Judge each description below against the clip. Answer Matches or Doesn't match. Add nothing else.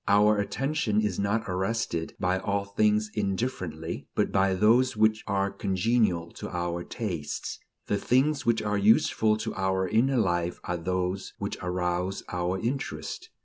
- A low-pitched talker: Matches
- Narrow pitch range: Doesn't match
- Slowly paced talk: Doesn't match